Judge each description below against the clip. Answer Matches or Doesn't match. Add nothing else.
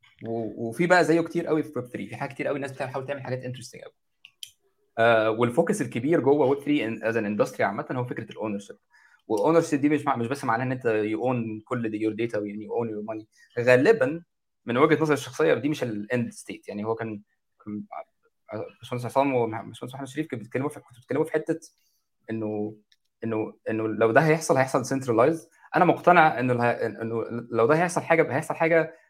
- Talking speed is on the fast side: Matches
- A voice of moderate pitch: Doesn't match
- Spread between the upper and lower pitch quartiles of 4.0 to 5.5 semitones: Matches